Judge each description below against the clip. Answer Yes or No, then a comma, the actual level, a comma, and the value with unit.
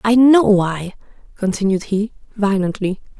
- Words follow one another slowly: Yes, slow, 115 wpm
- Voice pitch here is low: No, high, 205 Hz